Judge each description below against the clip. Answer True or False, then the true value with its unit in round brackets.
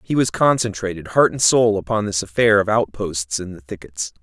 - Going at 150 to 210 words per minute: True (200 wpm)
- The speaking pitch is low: True (100 Hz)